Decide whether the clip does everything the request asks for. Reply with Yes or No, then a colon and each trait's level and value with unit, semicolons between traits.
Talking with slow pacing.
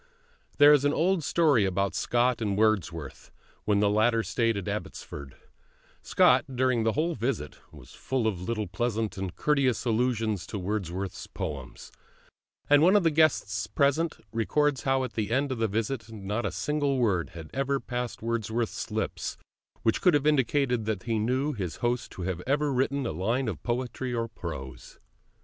No: average, 170 wpm